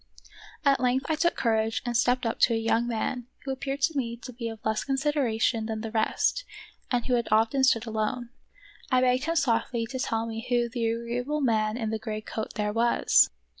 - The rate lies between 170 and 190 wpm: No, fast, 205 wpm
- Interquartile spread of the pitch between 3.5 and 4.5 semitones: No, narrow, 2.5 semitones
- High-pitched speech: Yes, high, 235 Hz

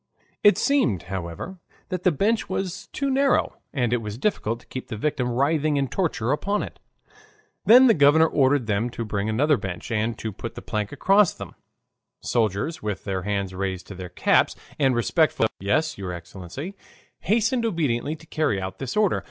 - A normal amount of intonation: No, wide, 8.4 semitones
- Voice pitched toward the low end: Yes, low, 130 Hz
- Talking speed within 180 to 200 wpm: Yes, average, 185 wpm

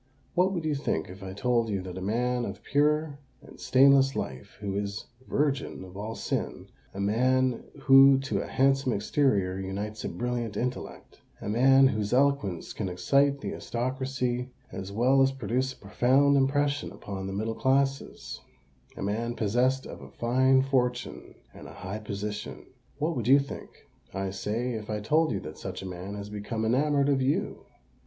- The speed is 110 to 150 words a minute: No, average, 165 wpm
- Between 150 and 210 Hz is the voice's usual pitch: No, low, 125 Hz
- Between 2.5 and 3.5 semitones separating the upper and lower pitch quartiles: No, average, 4.9 semitones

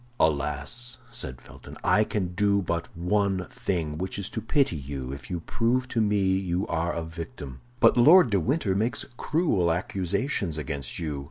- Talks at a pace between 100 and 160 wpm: No, average, 170 wpm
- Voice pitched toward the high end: No, very low, 95 Hz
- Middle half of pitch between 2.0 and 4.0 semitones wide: No, average, 5.0 semitones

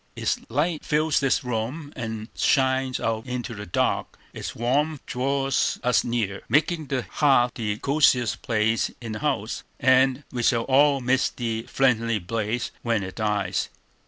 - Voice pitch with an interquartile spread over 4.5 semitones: No, average, 3.4 semitones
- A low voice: Yes, low, 125 Hz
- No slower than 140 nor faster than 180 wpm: Yes, average, 155 wpm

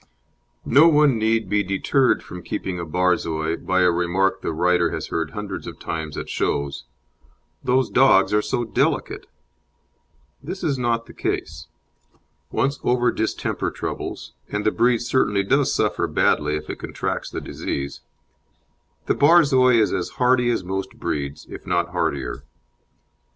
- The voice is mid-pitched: No, low, 100 Hz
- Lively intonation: Yes, wide, 6.6 semitones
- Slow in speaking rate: No, average, 150 wpm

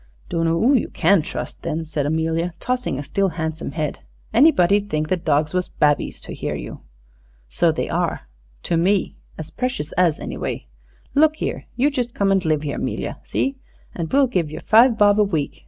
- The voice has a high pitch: No, medium, 175 Hz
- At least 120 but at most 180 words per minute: No, average, 190 wpm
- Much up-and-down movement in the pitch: Yes, wide, 5.9 semitones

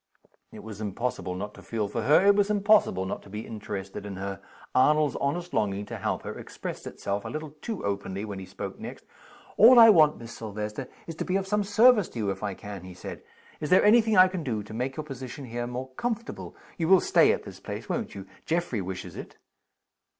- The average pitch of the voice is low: Yes, low, 125 Hz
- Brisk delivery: Yes, fast, 225 wpm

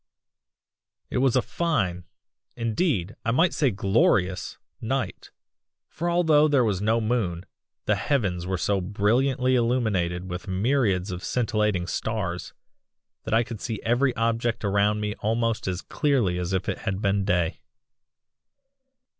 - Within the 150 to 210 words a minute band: No, average, 140 wpm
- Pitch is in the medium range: No, low, 110 Hz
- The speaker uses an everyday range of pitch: Yes, average, 4.6 semitones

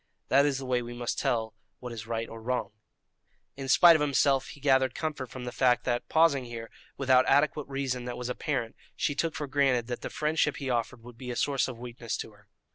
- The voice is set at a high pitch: No, low, 125 Hz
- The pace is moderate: No, fast, 225 wpm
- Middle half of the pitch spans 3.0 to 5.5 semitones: No, narrow, 2.6 semitones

